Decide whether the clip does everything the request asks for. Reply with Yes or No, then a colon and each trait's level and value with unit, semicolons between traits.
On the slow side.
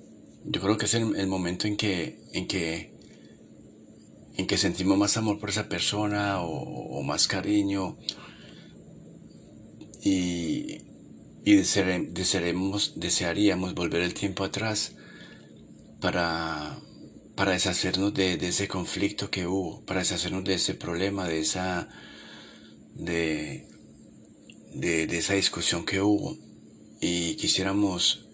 Yes: slow, 120 wpm